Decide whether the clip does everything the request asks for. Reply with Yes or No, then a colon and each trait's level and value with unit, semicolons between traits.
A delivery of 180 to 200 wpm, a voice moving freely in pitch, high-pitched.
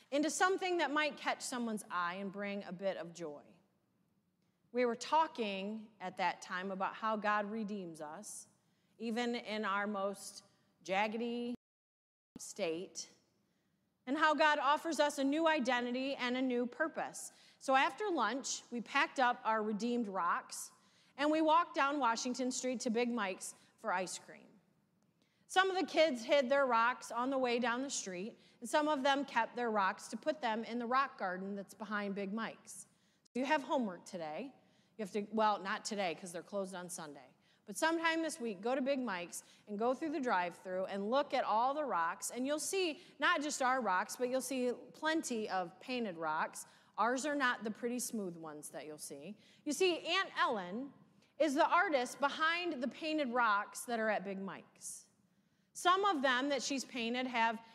Yes: average, 185 wpm; wide, 5.9 semitones; high, 230 Hz